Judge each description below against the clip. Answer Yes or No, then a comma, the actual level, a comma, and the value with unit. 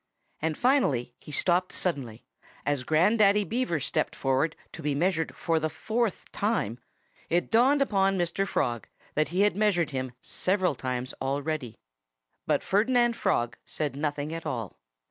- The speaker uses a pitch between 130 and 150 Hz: No, medium, 160 Hz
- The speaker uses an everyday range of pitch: No, wide, 6.4 semitones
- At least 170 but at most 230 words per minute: No, average, 145 wpm